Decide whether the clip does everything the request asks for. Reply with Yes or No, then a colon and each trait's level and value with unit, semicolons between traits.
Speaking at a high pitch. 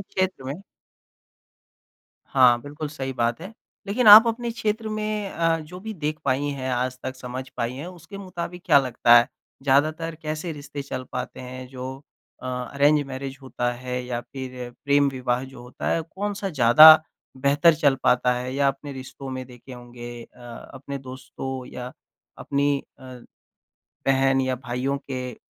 No: low, 135 Hz